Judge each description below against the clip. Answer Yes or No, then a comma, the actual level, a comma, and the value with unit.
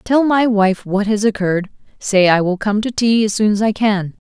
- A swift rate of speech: Yes, fast, 225 wpm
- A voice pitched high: Yes, high, 210 Hz